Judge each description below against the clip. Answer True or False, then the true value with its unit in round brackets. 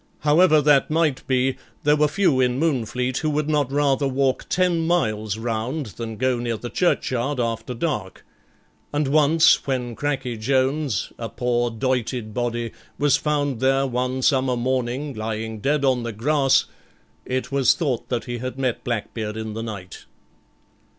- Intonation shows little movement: False (3.6 semitones)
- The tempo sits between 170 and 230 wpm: False (155 wpm)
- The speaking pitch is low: True (130 Hz)